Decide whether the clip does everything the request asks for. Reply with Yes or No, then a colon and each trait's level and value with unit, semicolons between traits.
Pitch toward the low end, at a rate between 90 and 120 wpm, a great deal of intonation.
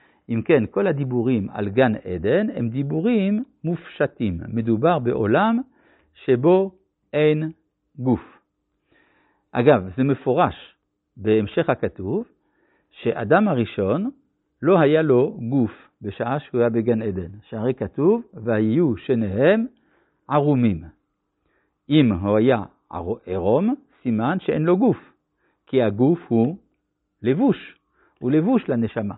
Yes: low, 130 Hz; average, 105 wpm; wide, 7.8 semitones